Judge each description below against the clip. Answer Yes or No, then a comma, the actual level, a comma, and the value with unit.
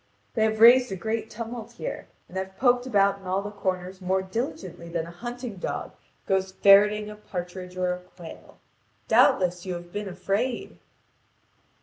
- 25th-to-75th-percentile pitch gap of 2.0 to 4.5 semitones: Yes, average, 3.4 semitones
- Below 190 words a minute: Yes, average, 165 wpm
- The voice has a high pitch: Yes, high, 195 Hz